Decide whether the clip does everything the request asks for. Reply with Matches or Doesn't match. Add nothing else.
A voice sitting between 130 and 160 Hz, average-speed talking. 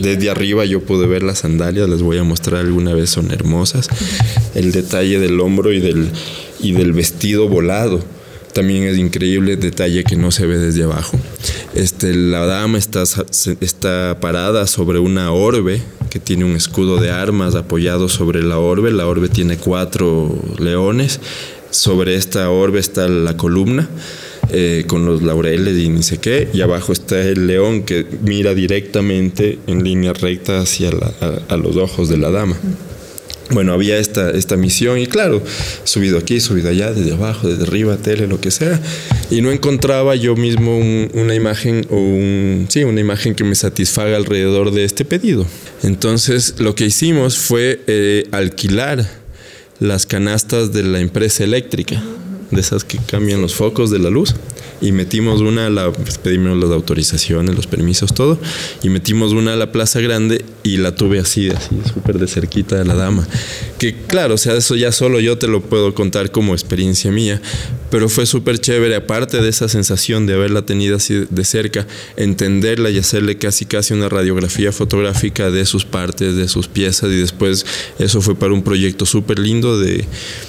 Doesn't match